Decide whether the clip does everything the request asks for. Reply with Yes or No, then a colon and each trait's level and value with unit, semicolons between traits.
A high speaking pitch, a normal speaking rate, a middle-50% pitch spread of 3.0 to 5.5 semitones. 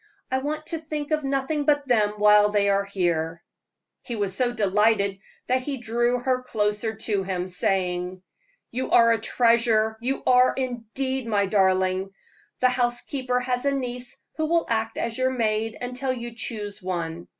Yes: high, 230 Hz; average, 165 wpm; average, 4.1 semitones